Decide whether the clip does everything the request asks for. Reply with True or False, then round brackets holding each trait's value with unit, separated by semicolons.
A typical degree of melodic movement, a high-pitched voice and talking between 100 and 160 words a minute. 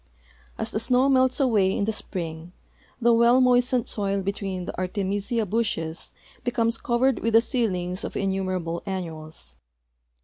True (4.5 semitones; 205 Hz; 140 wpm)